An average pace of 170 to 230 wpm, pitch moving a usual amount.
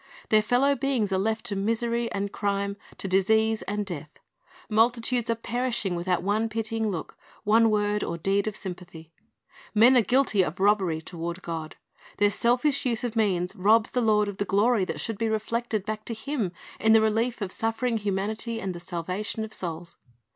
Yes: average, 185 wpm; average, 3.0 semitones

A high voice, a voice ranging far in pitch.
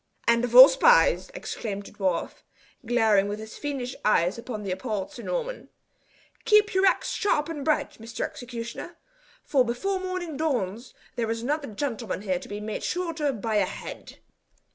Yes: high, 245 Hz; wide, 6.4 semitones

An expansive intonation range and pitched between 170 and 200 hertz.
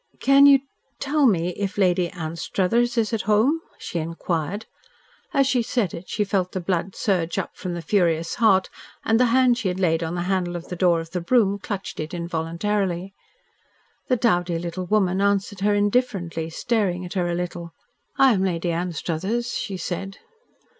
No: average, 3.7 semitones; medium, 185 Hz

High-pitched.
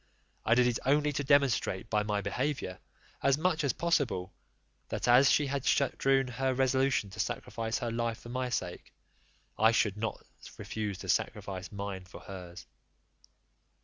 No: low, 120 Hz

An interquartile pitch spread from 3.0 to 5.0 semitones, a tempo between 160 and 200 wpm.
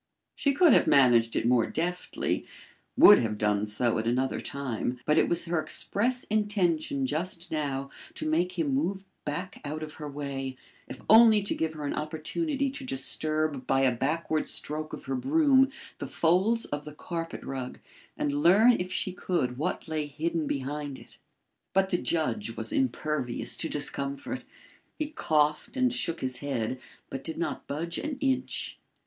No: wide, 5.6 semitones; average, 170 wpm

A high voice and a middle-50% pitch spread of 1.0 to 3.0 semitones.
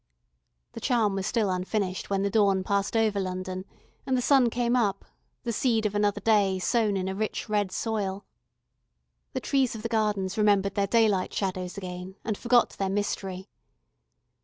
Yes: high, 205 Hz; average, 2.7 semitones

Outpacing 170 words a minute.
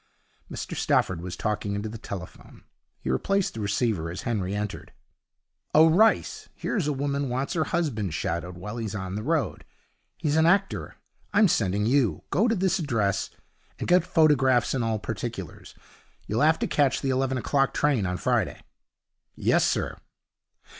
No: average, 160 wpm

